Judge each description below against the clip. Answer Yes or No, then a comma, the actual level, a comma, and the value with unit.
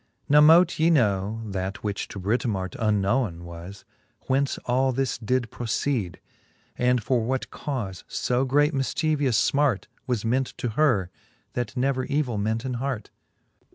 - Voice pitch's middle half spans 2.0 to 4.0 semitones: No, average, 4.5 semitones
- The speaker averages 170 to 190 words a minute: No, average, 145 wpm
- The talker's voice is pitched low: Yes, low, 125 Hz